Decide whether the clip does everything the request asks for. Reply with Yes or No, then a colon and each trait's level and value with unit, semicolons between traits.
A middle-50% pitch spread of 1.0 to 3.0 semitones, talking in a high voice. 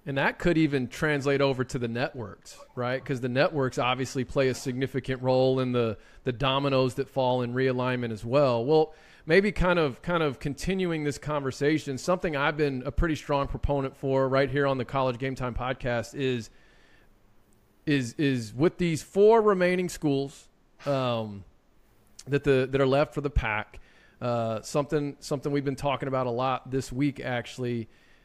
No: narrow, 2.6 semitones; low, 135 Hz